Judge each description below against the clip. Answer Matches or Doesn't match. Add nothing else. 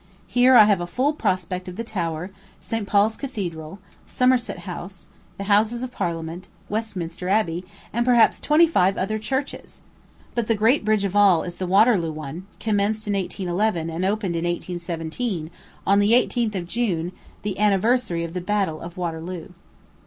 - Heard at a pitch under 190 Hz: Doesn't match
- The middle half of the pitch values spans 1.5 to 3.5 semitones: Doesn't match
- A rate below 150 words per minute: Doesn't match